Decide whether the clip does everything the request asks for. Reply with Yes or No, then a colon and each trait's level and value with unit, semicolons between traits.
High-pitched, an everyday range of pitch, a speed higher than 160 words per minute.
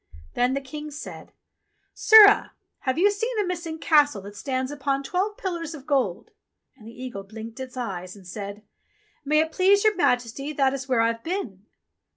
No: very high, 275 Hz; wide, 6.5 semitones; average, 185 wpm